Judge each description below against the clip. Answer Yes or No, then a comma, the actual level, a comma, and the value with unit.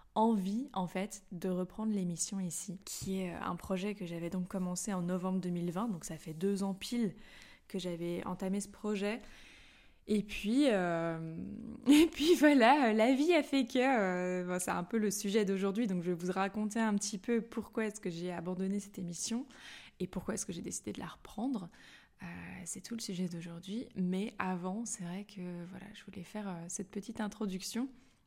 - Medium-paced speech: Yes, average, 190 wpm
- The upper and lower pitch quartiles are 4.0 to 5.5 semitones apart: No, average, 3.3 semitones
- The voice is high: Yes, high, 195 Hz